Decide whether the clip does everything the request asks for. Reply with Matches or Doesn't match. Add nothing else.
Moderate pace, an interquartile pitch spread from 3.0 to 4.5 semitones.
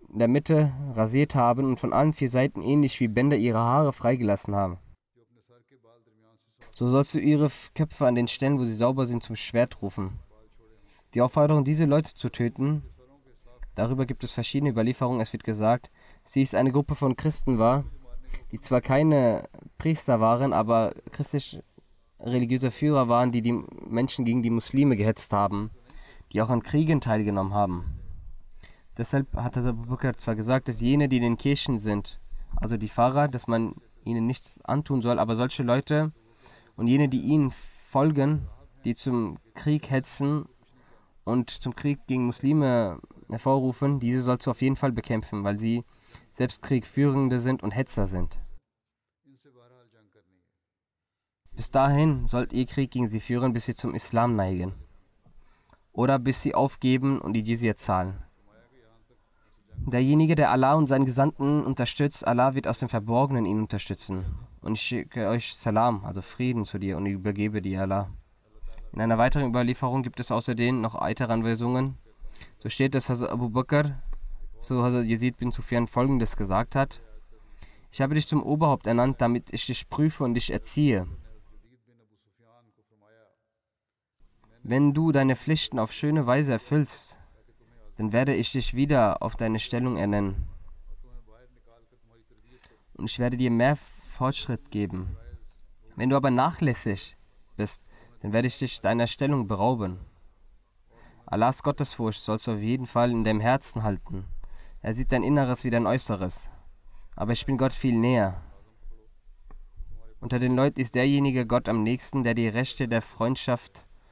Matches